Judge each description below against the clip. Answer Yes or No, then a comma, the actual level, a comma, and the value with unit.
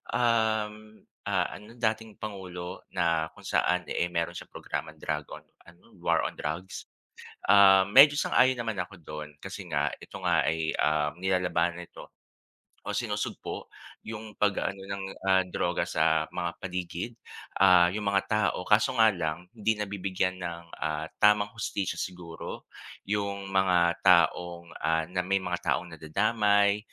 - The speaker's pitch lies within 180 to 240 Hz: No, very low, 95 Hz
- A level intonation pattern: No, average, 3.5 semitones